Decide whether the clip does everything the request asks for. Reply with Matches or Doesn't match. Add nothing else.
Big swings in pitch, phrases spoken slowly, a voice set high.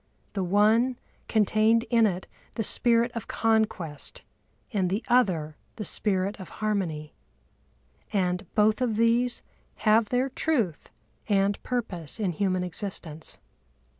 Doesn't match